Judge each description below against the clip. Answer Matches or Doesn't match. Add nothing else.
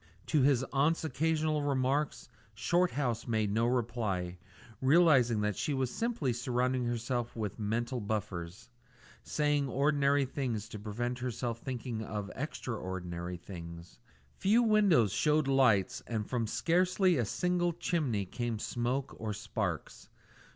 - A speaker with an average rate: Doesn't match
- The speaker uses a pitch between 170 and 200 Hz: Doesn't match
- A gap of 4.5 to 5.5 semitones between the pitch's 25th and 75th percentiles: Matches